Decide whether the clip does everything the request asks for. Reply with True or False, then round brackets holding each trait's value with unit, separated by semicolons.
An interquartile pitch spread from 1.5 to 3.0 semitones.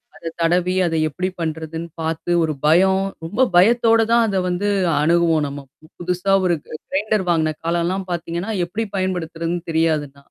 True (2.7 semitones)